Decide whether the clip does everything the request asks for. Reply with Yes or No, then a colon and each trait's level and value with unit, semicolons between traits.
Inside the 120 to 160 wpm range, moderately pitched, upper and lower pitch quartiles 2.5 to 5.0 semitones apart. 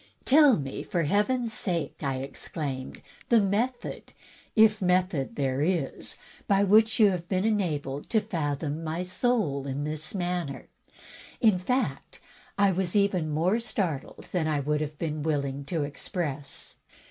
No: average, 150 wpm; medium, 175 Hz; wide, 5.6 semitones